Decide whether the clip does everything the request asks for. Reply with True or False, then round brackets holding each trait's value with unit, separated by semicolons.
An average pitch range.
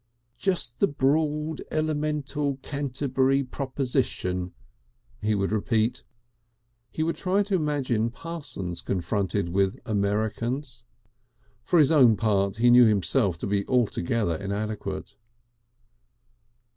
False (6.1 semitones)